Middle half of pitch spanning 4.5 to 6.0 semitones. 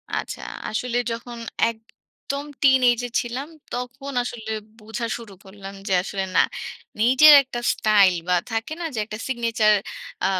No: average, 2.8 semitones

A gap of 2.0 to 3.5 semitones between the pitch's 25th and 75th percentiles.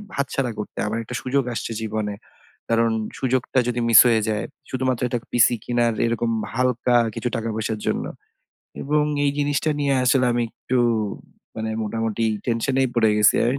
Yes: narrow, 2.4 semitones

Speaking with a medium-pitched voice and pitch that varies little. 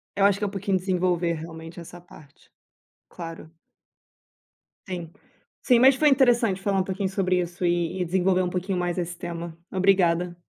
Yes: medium, 180 Hz; narrow, 2.2 semitones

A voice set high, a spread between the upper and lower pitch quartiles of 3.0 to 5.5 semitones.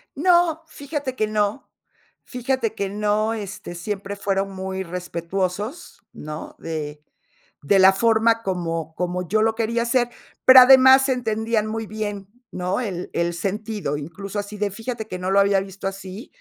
Yes: high, 205 Hz; average, 3.4 semitones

